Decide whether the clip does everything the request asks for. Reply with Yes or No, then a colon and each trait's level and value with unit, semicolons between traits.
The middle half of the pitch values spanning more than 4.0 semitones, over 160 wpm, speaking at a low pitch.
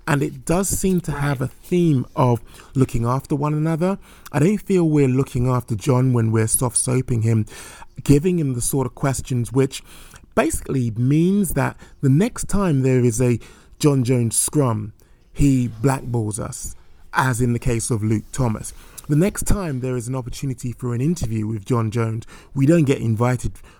No: average, 3.7 semitones; average, 180 wpm; low, 130 Hz